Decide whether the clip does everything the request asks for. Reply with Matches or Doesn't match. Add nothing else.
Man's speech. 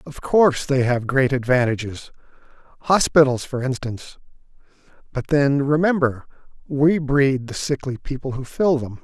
Matches